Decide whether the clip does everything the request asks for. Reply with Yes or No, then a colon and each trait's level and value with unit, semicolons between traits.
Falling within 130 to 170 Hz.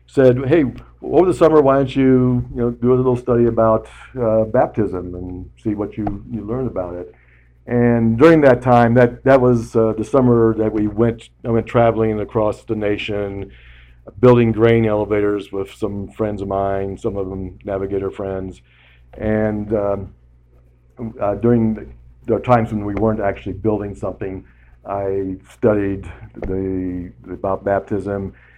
No: low, 105 Hz